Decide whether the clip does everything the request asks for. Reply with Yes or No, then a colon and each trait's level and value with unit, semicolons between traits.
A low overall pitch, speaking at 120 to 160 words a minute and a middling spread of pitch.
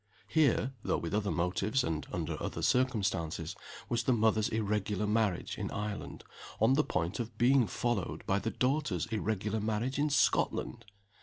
Yes: low, 110 Hz; average, 155 wpm; average, 3.5 semitones